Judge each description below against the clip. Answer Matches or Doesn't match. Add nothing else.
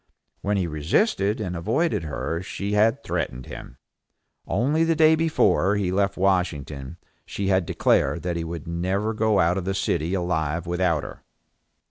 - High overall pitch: Doesn't match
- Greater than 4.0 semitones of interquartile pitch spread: Doesn't match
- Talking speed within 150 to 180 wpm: Matches